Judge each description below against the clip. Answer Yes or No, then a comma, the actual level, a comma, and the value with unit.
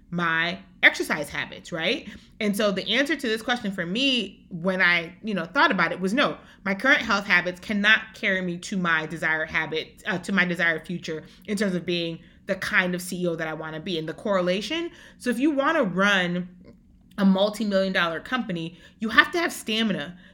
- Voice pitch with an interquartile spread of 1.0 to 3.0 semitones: No, average, 4.1 semitones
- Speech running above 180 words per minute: Yes, fast, 205 wpm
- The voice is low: No, high, 190 Hz